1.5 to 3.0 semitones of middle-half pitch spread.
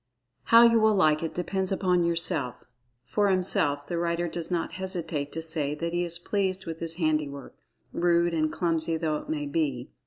Yes: narrow, 2.6 semitones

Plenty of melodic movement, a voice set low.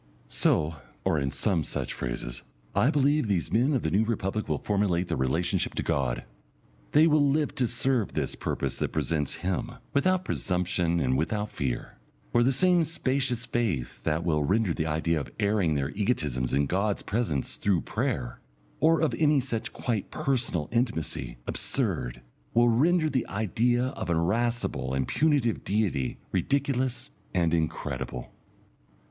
Yes: wide, 8.3 semitones; low, 105 Hz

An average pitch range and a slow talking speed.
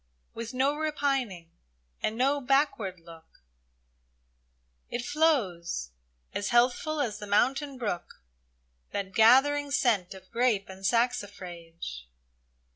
No: wide, 6.4 semitones; slow, 110 wpm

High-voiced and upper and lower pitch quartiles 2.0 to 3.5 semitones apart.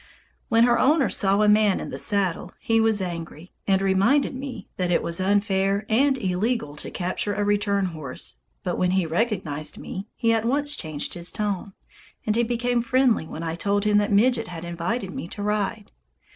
No: high, 205 Hz; average, 4.0 semitones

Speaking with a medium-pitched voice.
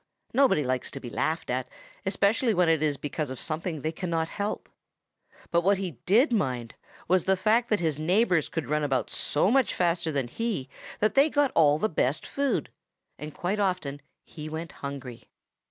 Yes: medium, 165 Hz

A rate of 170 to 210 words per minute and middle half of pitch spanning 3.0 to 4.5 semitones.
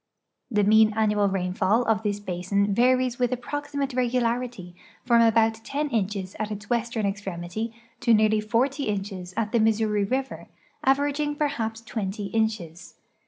No: slow, 135 wpm; average, 3.3 semitones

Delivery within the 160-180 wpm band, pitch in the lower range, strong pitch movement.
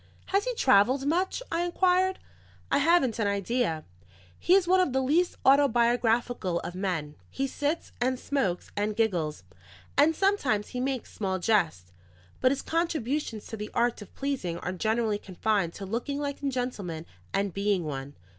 No: average, 165 wpm; high, 240 Hz; wide, 6.3 semitones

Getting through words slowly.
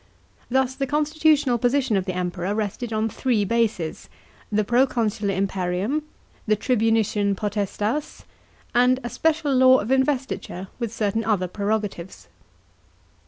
Yes: slow, 120 wpm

